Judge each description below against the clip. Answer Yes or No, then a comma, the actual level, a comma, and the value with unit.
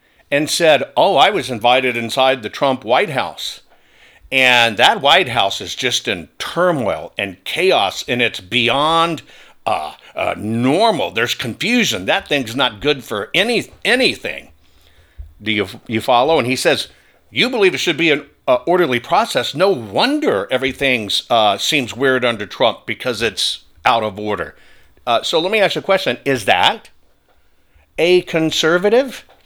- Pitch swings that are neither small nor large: No, wide, 6.6 semitones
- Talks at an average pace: Yes, average, 155 wpm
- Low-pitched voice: Yes, low, 130 Hz